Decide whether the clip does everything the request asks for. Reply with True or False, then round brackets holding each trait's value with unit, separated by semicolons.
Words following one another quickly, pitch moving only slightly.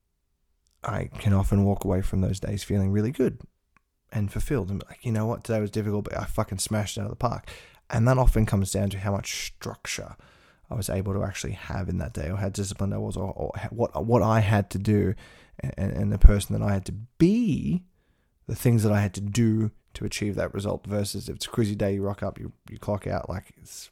True (245 wpm; 2.1 semitones)